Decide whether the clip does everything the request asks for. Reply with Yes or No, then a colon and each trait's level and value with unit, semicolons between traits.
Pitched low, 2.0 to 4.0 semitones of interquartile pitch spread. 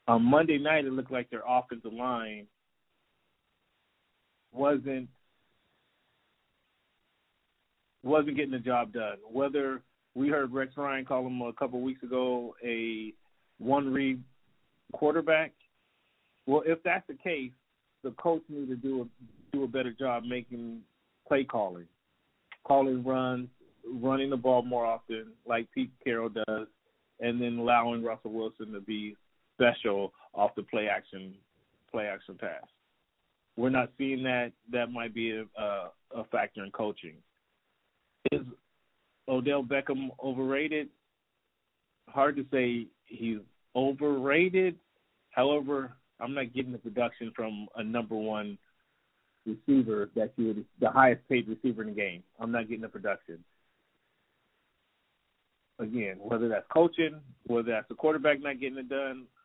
Yes: low, 125 Hz; average, 3.1 semitones